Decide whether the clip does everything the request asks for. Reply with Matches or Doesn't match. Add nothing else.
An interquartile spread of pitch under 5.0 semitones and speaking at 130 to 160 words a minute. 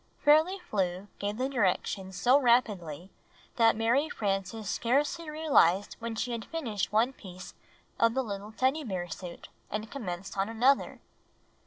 Doesn't match